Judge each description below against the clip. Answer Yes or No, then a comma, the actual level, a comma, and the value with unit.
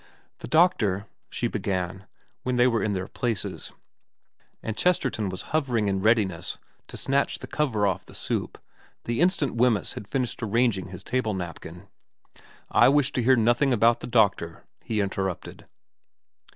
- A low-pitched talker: Yes, low, 110 Hz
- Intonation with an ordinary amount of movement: Yes, average, 4.6 semitones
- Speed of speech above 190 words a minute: No, average, 165 wpm